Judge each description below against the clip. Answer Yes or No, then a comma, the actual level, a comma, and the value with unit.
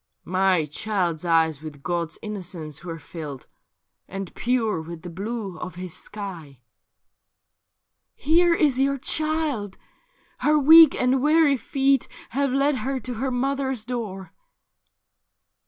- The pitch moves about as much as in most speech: No, wide, 8.0 semitones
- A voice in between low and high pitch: No, high, 215 Hz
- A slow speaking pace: Yes, slow, 130 wpm